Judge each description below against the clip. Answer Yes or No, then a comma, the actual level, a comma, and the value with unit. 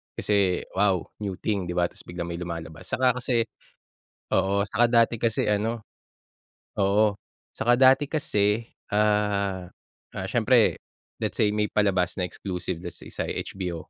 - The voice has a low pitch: Yes, low, 100 Hz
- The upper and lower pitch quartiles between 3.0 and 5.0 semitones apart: Yes, average, 3.4 semitones